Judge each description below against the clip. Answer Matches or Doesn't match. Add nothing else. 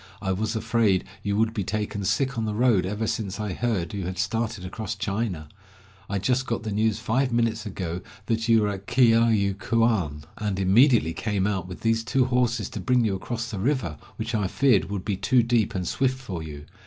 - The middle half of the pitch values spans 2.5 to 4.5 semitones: Matches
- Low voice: Matches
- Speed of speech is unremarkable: Doesn't match